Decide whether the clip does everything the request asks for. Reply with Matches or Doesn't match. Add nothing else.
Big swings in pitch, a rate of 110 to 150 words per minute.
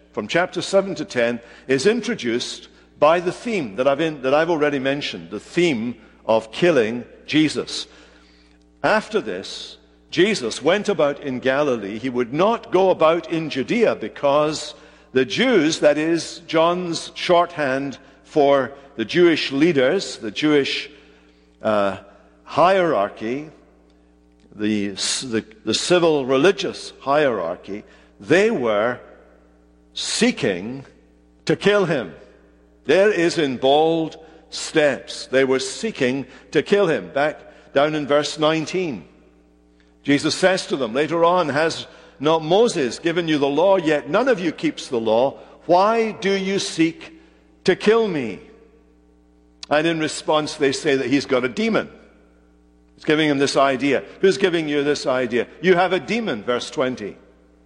Matches